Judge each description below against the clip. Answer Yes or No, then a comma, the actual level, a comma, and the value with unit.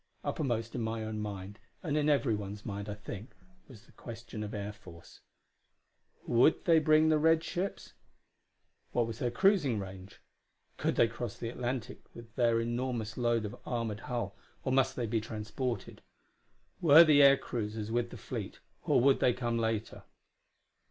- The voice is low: Yes, low, 115 Hz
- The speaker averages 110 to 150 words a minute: No, average, 165 wpm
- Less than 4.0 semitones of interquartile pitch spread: Yes, average, 3.5 semitones